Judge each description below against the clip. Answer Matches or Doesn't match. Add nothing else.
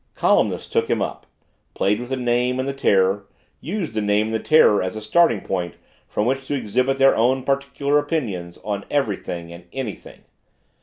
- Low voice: Matches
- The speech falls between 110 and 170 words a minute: Doesn't match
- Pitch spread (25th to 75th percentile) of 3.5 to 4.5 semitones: Doesn't match